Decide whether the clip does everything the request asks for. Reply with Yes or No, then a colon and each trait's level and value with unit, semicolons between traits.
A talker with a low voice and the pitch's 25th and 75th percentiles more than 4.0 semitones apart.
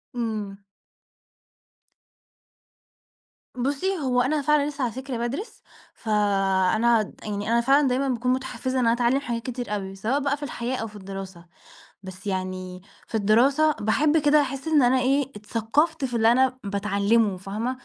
No: high, 240 Hz; average, 4.7 semitones